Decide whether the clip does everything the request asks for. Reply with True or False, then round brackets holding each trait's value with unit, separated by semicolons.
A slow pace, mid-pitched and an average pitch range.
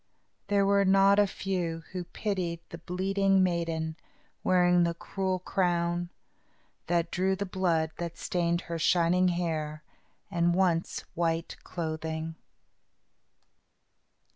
False (115 wpm; 175 Hz; 2.1 semitones)